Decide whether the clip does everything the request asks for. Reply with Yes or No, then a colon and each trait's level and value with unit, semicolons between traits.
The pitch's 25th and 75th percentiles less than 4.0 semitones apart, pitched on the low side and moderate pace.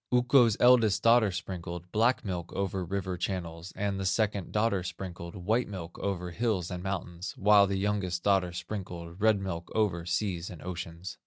Yes: average, 3.0 semitones; very low, 95 Hz; average, 165 wpm